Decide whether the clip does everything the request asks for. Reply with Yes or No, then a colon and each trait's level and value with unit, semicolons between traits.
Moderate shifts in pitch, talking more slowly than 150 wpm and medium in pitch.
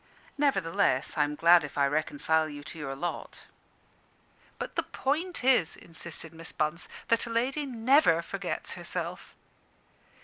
No: wide, 8.7 semitones; average, 140 wpm; medium, 165 Hz